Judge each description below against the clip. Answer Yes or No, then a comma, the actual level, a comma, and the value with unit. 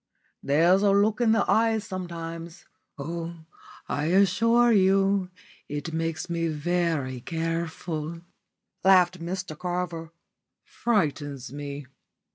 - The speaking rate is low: Yes, slow, 100 wpm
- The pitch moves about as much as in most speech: Yes, average, 3.3 semitones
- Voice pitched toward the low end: No, medium, 170 Hz